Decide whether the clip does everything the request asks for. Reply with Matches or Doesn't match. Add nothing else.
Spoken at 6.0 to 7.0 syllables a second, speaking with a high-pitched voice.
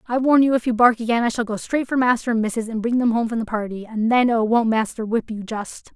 Matches